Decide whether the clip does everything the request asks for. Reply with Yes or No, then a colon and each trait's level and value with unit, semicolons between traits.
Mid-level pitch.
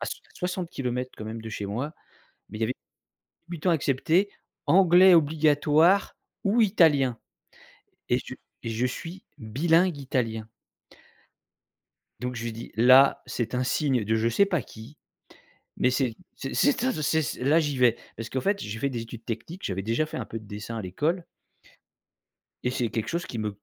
No: low, 130 Hz